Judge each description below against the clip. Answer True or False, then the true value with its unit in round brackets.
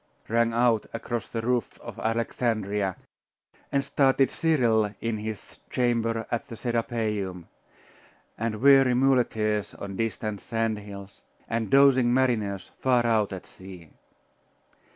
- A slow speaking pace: True (120 wpm)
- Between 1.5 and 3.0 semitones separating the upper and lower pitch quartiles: True (2.7 semitones)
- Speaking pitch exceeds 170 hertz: False (115 Hz)